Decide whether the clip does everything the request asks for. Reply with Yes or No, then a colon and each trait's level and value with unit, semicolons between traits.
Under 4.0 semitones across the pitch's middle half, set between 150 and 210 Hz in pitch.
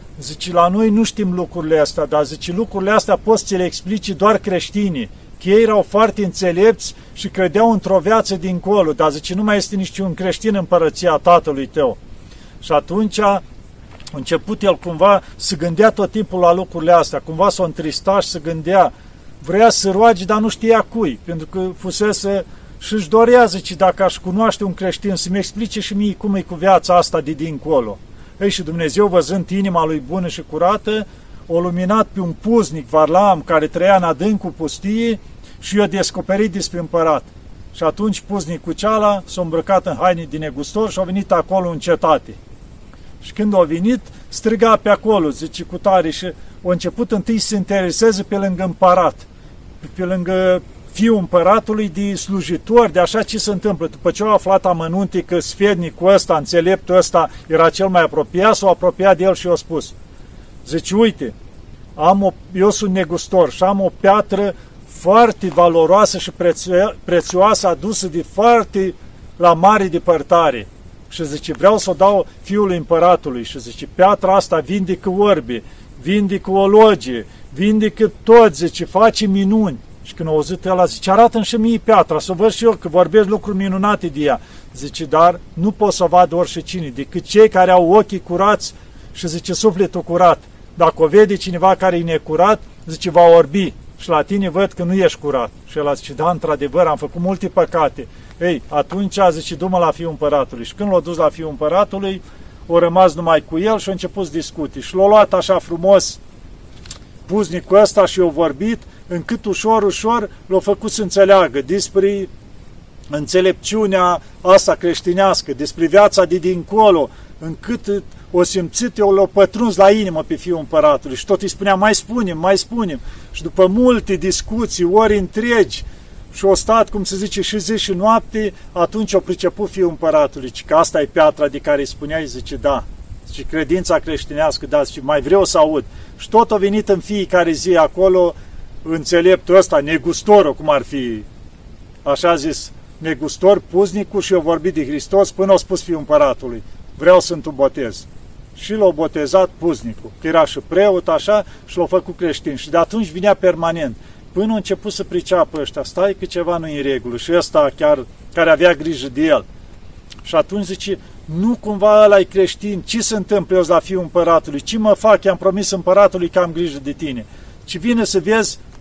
Yes: average, 3.5 semitones; medium, 185 Hz